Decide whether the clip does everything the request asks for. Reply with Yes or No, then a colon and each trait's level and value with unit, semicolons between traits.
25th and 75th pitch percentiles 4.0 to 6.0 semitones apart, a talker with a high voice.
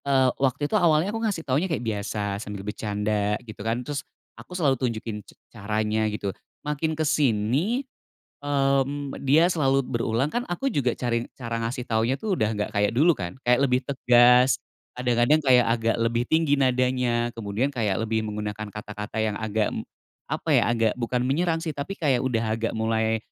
No: average, 4.3 semitones; low, 120 Hz